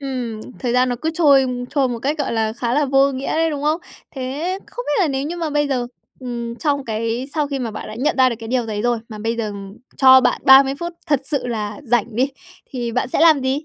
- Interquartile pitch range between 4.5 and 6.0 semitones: No, average, 3.5 semitones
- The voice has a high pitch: Yes, very high, 260 Hz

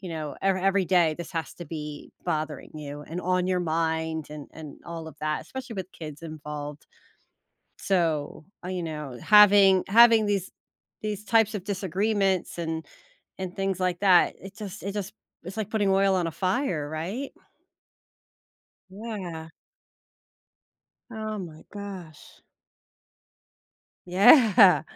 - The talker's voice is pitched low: No, medium, 185 Hz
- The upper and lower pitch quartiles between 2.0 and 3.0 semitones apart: No, average, 3.9 semitones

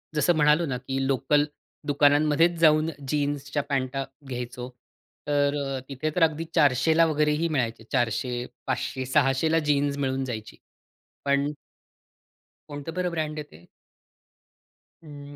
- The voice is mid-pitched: Yes, medium, 145 Hz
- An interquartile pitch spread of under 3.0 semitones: Yes, narrow, 2.6 semitones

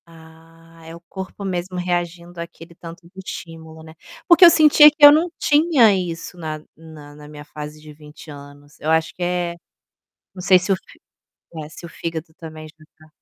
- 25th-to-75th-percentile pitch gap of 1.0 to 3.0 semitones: Yes, narrow, 2.5 semitones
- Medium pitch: Yes, medium, 165 Hz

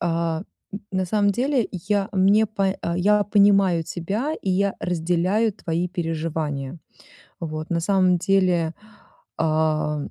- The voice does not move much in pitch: No, average, 3.5 semitones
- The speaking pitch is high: No, medium, 180 Hz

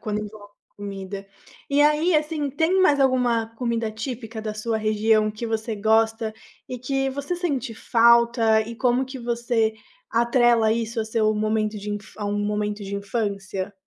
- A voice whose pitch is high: Yes, high, 225 Hz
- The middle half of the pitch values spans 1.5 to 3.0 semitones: Yes, average, 2.7 semitones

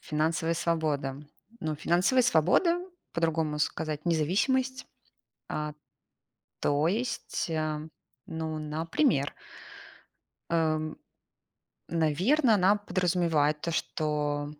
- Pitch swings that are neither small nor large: Yes, average, 3.3 semitones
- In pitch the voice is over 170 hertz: No, medium, 160 Hz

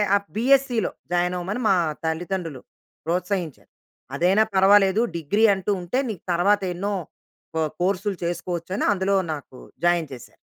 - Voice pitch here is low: No, medium, 185 Hz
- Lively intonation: No, average, 2.9 semitones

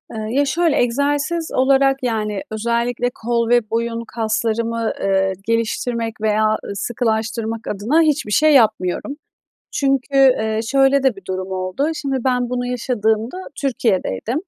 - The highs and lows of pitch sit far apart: No, average, 3.7 semitones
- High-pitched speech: Yes, high, 235 Hz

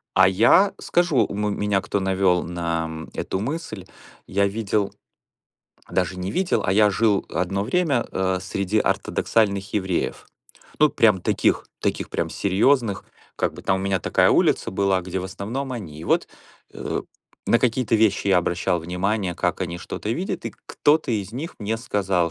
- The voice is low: Yes, low, 100 Hz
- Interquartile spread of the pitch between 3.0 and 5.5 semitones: Yes, average, 3.4 semitones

